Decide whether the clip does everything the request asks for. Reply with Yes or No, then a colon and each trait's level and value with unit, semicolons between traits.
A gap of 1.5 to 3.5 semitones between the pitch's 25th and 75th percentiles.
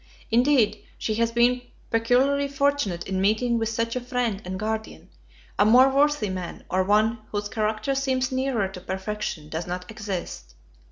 No: average, 4.4 semitones